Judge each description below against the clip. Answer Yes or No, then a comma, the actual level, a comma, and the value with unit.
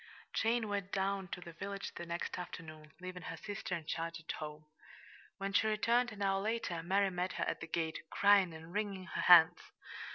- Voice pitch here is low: No, medium, 185 Hz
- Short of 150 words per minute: No, average, 195 wpm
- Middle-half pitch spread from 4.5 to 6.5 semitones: No, average, 3.2 semitones